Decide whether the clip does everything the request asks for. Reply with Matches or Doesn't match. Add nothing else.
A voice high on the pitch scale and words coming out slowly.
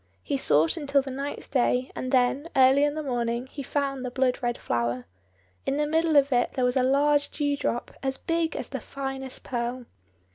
Doesn't match